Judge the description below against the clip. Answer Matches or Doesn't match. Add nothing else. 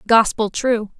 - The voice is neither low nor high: Doesn't match